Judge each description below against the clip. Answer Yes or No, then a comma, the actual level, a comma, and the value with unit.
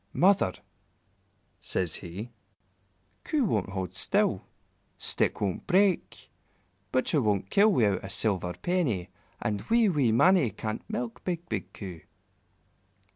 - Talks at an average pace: No, slow, 120 wpm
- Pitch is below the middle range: Yes, low, 110 Hz